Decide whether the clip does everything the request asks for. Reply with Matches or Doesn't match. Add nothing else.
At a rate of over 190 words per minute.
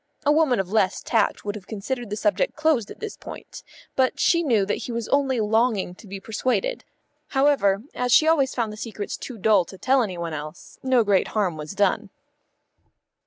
Matches